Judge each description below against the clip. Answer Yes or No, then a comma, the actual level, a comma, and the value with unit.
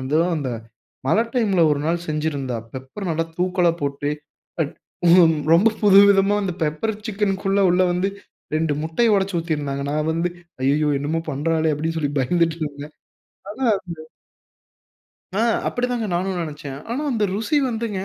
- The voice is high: No, medium, 165 Hz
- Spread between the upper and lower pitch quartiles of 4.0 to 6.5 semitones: Yes, average, 4.6 semitones